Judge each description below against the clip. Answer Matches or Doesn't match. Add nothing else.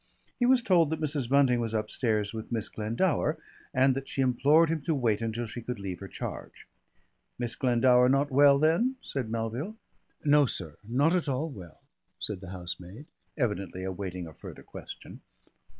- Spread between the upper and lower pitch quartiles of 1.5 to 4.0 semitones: Doesn't match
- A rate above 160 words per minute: Matches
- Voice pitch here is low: Matches